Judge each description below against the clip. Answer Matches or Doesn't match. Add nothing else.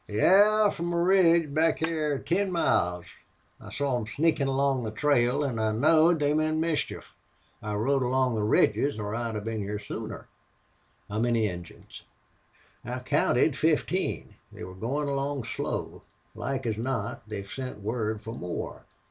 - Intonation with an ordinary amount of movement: Doesn't match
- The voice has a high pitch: Doesn't match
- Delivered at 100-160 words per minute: Matches